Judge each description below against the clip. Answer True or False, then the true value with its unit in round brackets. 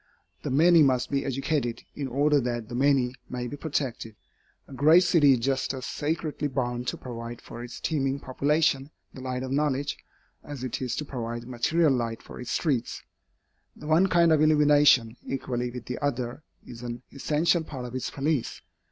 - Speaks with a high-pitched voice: False (135 Hz)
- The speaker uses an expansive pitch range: False (3.3 semitones)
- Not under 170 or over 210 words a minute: True (180 wpm)